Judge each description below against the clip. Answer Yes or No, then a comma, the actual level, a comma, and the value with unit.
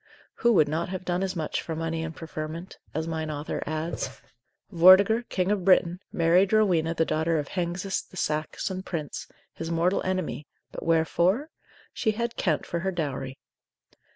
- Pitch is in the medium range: Yes, medium, 170 Hz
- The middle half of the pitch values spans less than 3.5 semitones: Yes, average, 2.8 semitones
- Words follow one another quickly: No, average, 165 wpm